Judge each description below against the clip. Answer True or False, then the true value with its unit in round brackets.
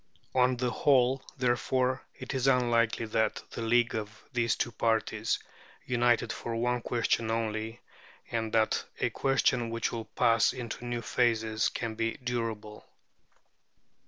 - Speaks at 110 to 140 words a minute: True (135 wpm)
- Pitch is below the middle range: True (115 Hz)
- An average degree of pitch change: False (1.6 semitones)